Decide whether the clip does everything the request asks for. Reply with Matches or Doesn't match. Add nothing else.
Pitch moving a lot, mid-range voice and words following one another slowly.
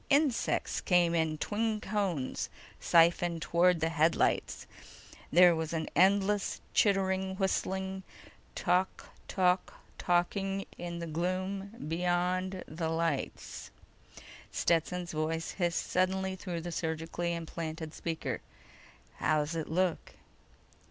Doesn't match